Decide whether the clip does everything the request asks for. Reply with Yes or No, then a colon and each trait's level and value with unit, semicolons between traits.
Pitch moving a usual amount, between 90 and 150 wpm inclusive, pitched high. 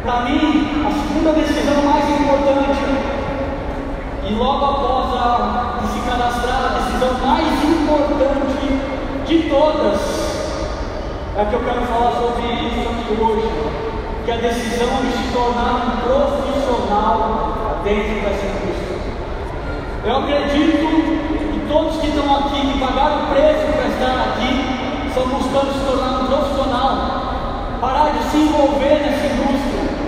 Yes: average, 3.1 semitones; average, 130 wpm; very high, 275 Hz